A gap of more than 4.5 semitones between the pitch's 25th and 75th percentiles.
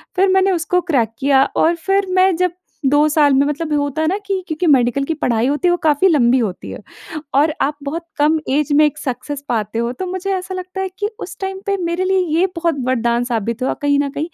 Yes: average, 5.2 semitones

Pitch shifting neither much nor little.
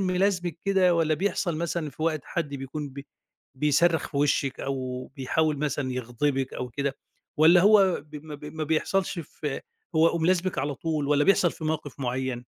Yes: average, 3.6 semitones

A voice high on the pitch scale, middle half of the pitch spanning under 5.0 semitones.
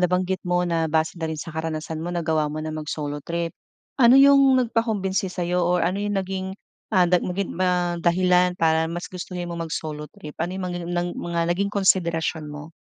No: medium, 175 Hz; narrow, 2.4 semitones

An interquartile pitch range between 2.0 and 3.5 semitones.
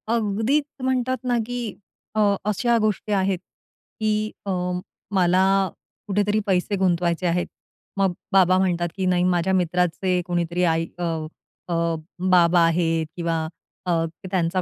Yes: average, 3.1 semitones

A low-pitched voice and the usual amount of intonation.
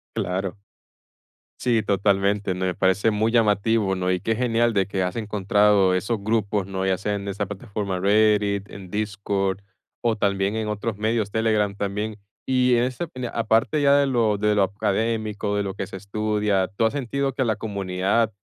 No: low, 105 Hz; narrow, 2.2 semitones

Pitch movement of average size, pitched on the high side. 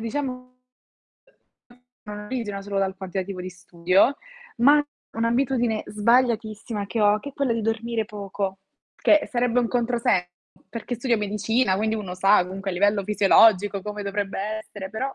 Yes: average, 3.2 semitones; high, 210 Hz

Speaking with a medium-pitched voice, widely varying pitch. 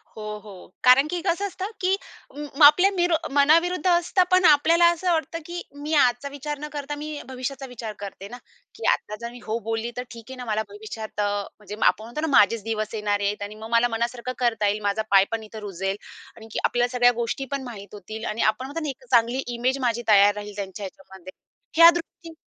No: high, 240 Hz; wide, 5.7 semitones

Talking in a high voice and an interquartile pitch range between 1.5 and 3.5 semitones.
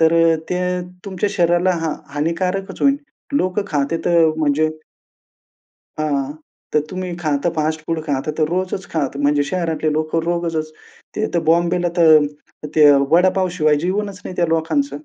No: medium, 165 Hz; average, 3.0 semitones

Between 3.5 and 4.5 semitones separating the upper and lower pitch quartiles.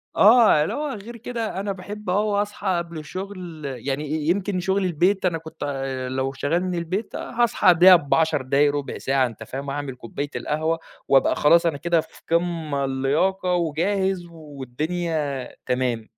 No: average, 5.1 semitones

